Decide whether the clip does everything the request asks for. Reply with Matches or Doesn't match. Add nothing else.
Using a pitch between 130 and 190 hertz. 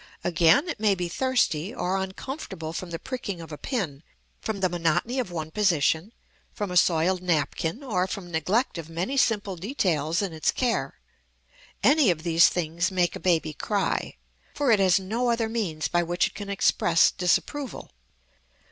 Matches